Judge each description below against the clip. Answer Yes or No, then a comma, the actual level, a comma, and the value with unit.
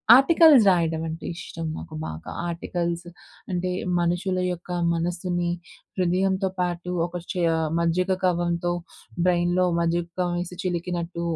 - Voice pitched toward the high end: No, medium, 175 Hz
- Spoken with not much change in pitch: Yes, narrow, 1.2 semitones